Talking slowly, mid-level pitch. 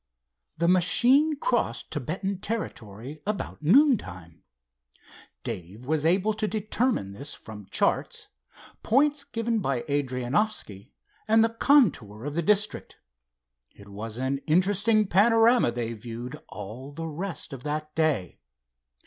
Yes: slow, 125 wpm; medium, 155 Hz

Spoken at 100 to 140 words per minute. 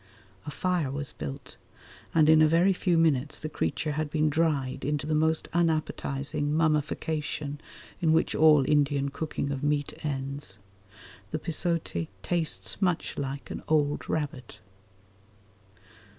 Yes: slow, 135 wpm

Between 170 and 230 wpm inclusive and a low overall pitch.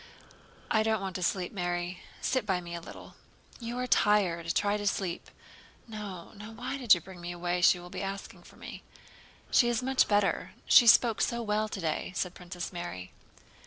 No: average, 185 wpm; high, 195 Hz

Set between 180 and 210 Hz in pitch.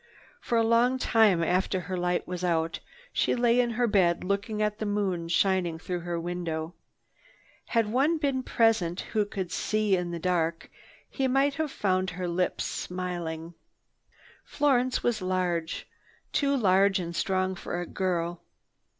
Yes: medium, 185 Hz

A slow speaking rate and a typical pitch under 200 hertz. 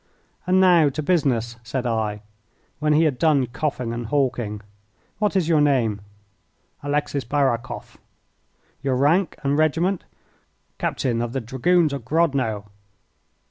Yes: slow, 130 wpm; medium, 140 Hz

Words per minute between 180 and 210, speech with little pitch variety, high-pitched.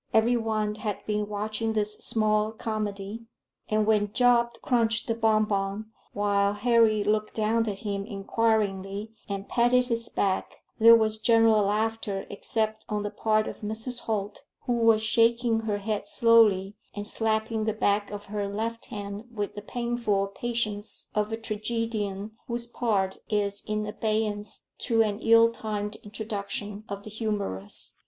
No: average, 150 wpm; narrow, 1.7 semitones; high, 215 Hz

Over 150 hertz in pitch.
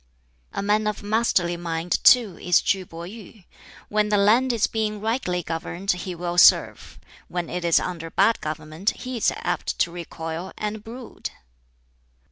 Yes: high, 190 Hz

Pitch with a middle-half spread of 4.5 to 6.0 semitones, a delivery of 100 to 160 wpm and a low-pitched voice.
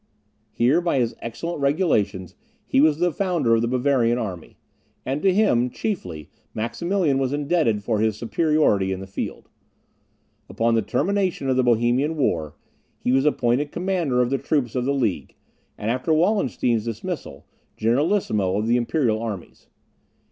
Yes: wide, 5.5 semitones; average, 155 wpm; low, 125 Hz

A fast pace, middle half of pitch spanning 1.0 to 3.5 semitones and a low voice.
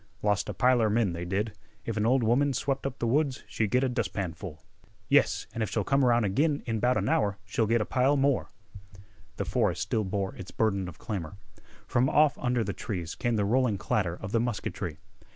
No: fast, 210 wpm; average, 4.3 semitones; low, 115 Hz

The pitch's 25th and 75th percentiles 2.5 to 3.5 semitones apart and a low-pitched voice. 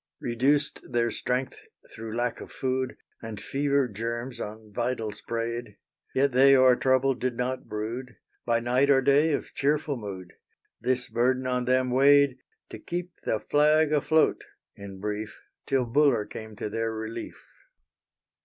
Yes: average, 3.2 semitones; low, 125 Hz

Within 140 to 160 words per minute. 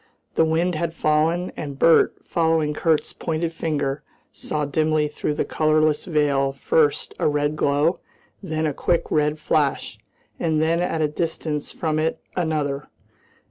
Yes: average, 150 wpm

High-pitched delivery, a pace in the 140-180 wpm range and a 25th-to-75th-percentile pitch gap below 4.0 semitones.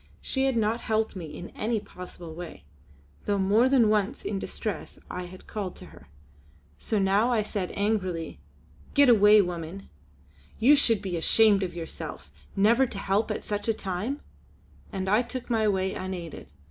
Yes: high, 205 Hz; average, 170 wpm; average, 3.2 semitones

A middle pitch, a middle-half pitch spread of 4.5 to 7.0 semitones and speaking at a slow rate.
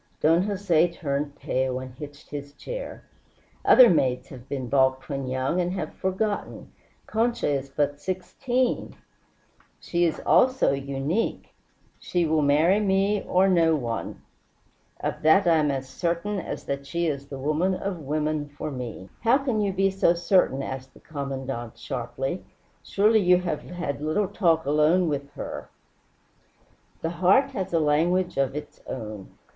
No: medium, 155 Hz; average, 5.1 semitones; average, 155 wpm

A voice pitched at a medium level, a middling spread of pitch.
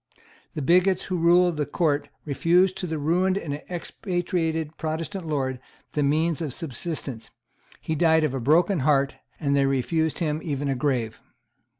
Yes: medium, 160 Hz; average, 3.4 semitones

